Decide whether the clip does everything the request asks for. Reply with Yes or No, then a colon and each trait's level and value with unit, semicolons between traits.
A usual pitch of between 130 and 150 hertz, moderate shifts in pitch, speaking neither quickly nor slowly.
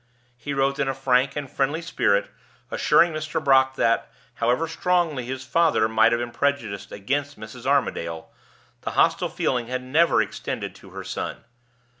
Yes: low, 135 Hz; average, 3.4 semitones; average, 160 wpm